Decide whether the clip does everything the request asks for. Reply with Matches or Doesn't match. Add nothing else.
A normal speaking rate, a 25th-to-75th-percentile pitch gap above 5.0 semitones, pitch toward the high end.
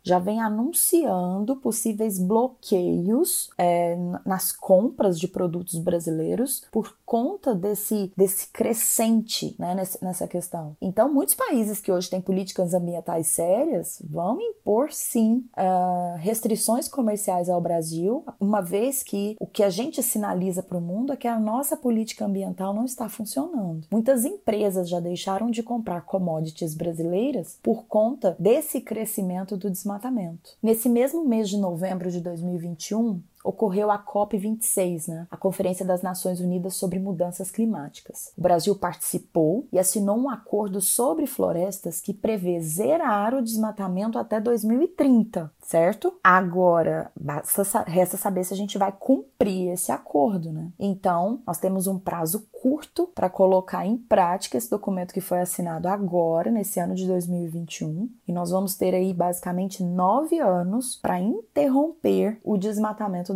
Doesn't match